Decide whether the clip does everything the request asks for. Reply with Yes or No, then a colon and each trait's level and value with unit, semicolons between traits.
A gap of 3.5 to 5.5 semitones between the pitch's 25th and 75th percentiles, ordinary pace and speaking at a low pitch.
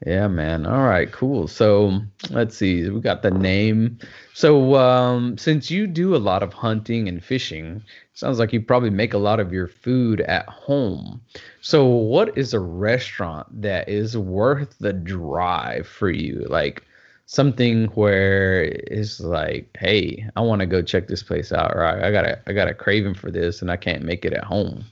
Yes: average, 4.1 semitones; average, 190 wpm; low, 105 Hz